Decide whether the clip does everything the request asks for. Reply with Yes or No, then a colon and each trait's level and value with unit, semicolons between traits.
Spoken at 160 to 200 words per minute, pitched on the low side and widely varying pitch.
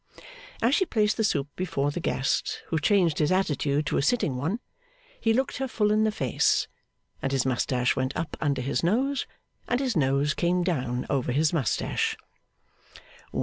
No: average, 175 wpm; medium, 160 Hz; wide, 7.5 semitones